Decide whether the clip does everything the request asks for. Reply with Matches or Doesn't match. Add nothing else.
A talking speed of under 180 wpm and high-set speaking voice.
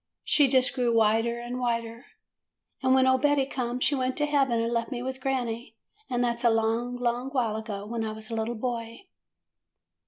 Doesn't match